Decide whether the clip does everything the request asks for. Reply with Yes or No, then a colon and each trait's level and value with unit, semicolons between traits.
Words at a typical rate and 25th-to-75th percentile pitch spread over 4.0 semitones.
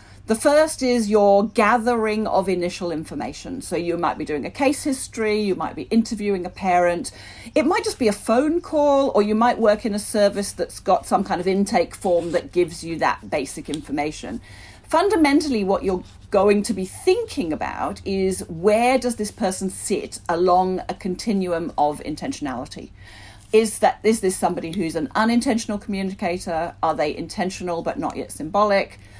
Yes: average, 175 wpm; average, 4.9 semitones